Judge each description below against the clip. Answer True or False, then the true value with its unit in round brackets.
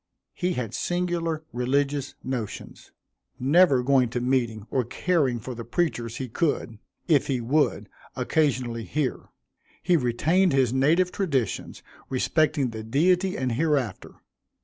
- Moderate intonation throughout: True (4.9 semitones)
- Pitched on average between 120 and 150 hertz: True (135 Hz)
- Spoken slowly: True (125 wpm)